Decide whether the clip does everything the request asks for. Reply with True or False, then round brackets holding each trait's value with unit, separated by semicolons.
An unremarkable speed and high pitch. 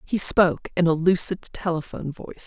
False (170 wpm; 175 Hz)